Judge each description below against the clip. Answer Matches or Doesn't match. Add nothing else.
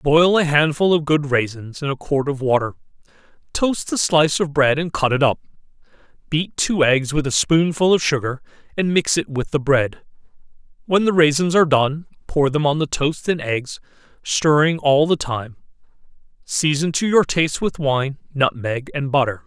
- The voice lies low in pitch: Doesn't match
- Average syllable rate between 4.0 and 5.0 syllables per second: Matches